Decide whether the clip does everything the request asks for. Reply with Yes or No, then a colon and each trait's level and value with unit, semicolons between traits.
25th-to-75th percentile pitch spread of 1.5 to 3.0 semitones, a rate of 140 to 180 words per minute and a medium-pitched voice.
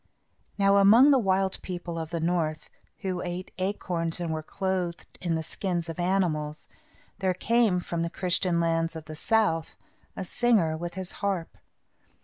Yes: average, 2.7 semitones; average, 160 wpm; medium, 175 Hz